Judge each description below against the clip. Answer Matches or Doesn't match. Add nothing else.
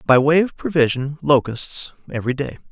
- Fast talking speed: Doesn't match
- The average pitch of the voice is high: Doesn't match